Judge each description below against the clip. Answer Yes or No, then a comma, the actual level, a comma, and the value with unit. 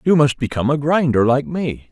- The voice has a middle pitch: Yes, medium, 145 Hz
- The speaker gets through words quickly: Yes, fast, 220 wpm